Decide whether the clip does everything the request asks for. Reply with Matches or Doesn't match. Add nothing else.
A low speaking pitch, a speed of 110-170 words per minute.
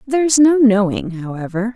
Doesn't match